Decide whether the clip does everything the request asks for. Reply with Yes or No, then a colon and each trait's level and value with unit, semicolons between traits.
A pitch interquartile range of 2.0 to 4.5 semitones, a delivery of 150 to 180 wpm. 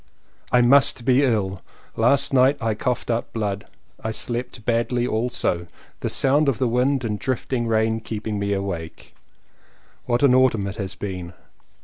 Yes: average, 3.4 semitones; average, 155 wpm